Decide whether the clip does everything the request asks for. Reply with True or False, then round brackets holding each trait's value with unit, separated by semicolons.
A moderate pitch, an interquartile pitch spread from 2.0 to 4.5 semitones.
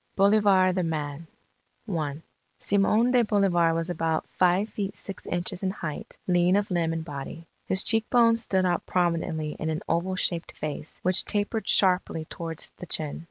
True (180 Hz; 3.4 semitones)